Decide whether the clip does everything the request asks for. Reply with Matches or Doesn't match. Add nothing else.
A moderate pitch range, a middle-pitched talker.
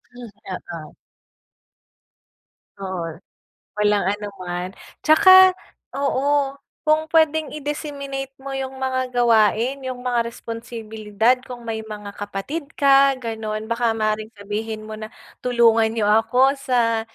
Doesn't match